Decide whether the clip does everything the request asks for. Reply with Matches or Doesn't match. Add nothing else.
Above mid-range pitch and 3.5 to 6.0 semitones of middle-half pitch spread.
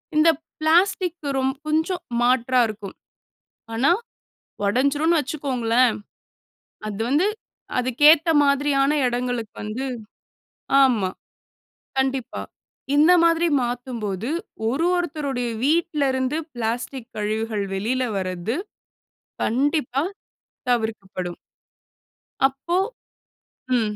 Matches